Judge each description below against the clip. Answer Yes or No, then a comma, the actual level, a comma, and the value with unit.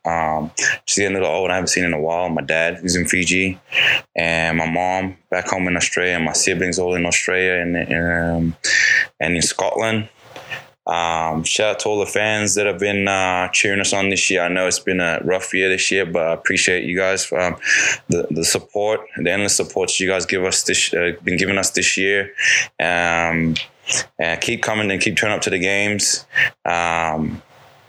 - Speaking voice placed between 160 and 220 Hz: No, very low, 90 Hz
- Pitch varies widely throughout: No, narrow, 2.6 semitones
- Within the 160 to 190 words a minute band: No, fast, 205 wpm